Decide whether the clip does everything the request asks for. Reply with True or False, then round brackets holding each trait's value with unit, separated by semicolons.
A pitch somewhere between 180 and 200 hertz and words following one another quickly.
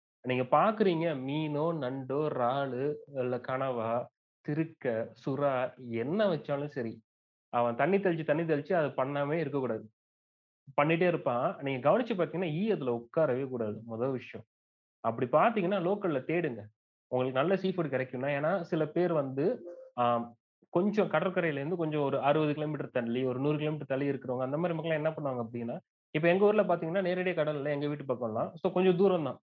False (145 Hz; 150 wpm)